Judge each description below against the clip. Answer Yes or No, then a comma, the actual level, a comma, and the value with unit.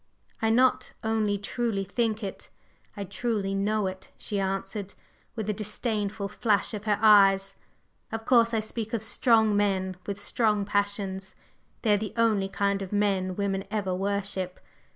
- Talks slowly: No, average, 155 wpm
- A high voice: Yes, high, 205 Hz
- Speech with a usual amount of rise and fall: No, narrow, 2.0 semitones